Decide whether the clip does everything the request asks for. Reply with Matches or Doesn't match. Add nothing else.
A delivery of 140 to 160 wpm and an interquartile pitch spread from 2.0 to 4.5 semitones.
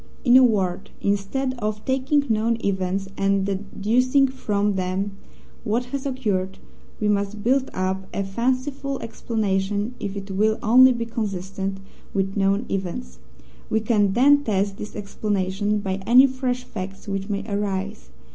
Matches